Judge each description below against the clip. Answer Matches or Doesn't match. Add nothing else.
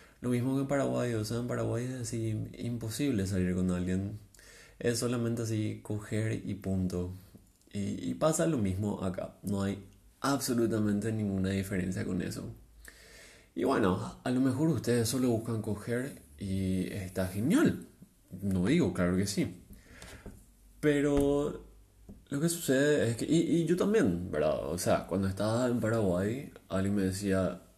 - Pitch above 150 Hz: Doesn't match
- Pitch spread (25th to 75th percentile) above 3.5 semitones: Matches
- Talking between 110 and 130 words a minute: Doesn't match